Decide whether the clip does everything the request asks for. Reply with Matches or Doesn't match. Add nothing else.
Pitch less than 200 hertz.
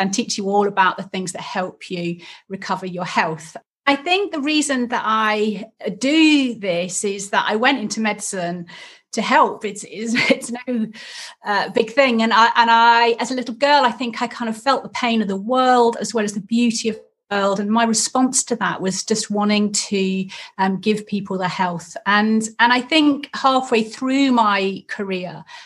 Doesn't match